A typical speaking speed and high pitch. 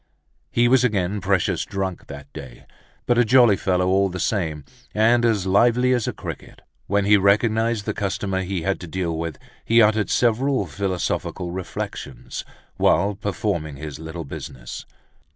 No: average, 155 wpm; low, 100 Hz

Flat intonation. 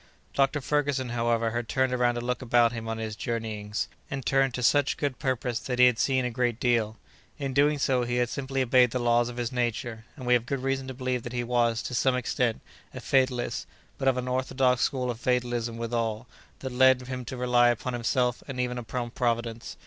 Yes: narrow, 1.7 semitones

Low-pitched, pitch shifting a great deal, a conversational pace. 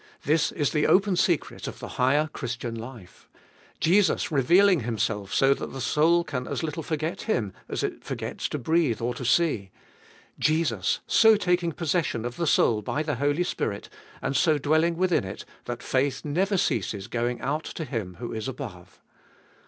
No: medium, 145 Hz; wide, 5.9 semitones; average, 175 wpm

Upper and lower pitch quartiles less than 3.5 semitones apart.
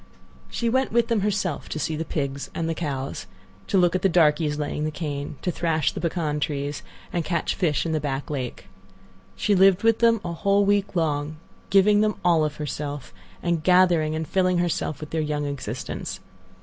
No: average, 3.9 semitones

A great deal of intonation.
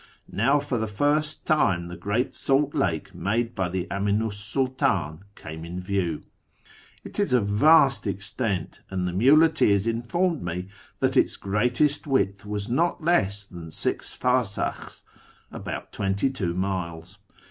Yes: wide, 6.2 semitones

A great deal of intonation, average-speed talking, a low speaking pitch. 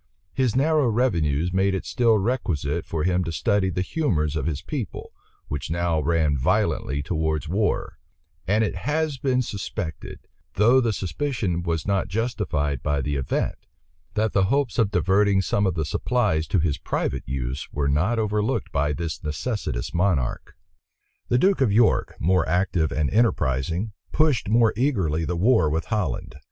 Yes: wide, 6.4 semitones; average, 160 wpm; very low, 95 Hz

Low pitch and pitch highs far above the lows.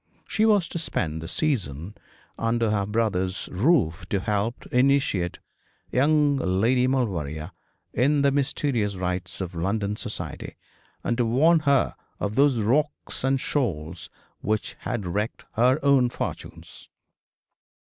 Yes: low, 115 Hz; wide, 6.6 semitones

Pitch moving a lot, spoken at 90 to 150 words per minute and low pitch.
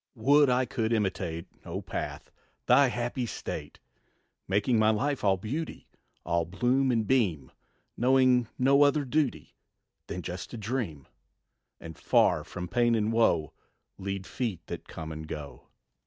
Yes: wide, 6.0 semitones; average, 140 wpm; low, 115 Hz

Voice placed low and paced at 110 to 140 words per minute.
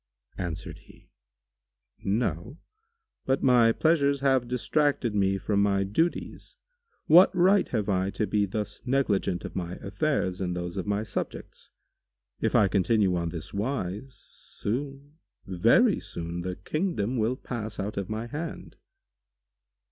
Yes: low, 105 Hz; slow, 135 wpm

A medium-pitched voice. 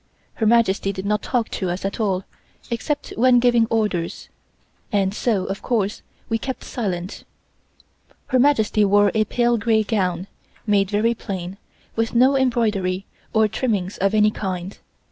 No: high, 210 Hz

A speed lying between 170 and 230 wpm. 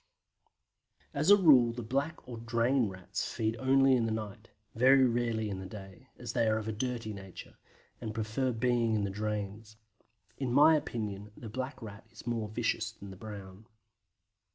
Yes: average, 175 wpm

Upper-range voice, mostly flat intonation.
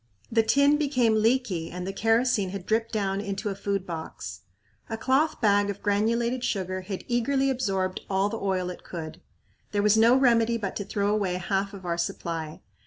No: high, 205 Hz; average, 3.6 semitones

